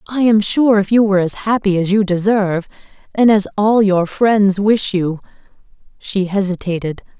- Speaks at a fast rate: No, average, 165 wpm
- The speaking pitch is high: Yes, high, 200 Hz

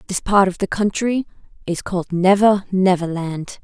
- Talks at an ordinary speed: Yes, average, 165 wpm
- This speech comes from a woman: Yes, female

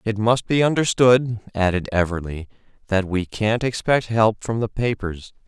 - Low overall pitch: Yes, low, 110 Hz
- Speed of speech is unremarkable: Yes, average, 155 wpm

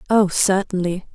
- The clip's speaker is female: Yes, female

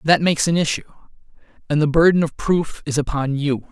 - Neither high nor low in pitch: Yes, medium, 155 Hz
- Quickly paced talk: No, average, 195 wpm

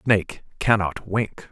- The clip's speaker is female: No, male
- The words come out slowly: Yes, slow, 120 wpm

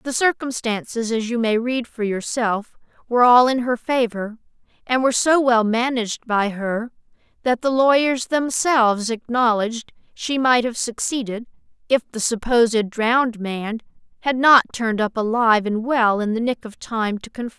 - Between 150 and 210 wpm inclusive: Yes, average, 165 wpm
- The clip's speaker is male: No, female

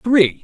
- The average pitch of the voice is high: Yes, high, 195 Hz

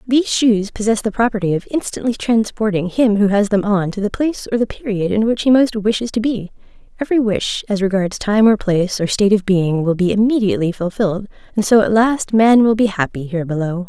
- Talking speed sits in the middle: No, fast, 220 wpm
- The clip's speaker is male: No, female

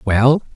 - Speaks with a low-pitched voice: Yes, low, 125 Hz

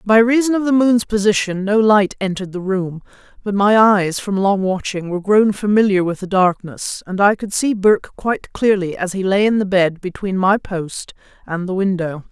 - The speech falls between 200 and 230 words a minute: Yes, fast, 205 wpm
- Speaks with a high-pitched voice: Yes, high, 200 Hz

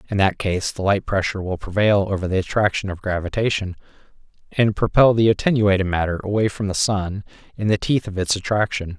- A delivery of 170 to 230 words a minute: Yes, average, 185 wpm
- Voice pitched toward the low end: Yes, low, 100 Hz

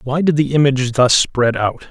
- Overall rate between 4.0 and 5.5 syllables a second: Yes, 5.0 syllables/s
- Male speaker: Yes, male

